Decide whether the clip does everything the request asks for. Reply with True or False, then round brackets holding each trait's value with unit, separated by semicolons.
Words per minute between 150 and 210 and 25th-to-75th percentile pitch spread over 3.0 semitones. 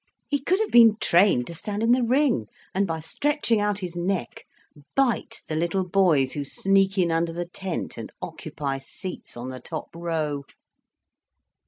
True (170 wpm; 4.5 semitones)